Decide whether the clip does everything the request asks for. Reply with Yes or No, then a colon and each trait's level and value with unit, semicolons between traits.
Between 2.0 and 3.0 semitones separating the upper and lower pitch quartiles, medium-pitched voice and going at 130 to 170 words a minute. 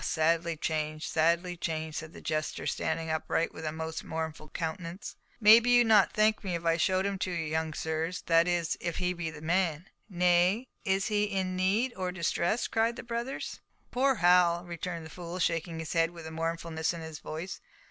No: average, 2.7 semitones; medium, 170 Hz; average, 190 wpm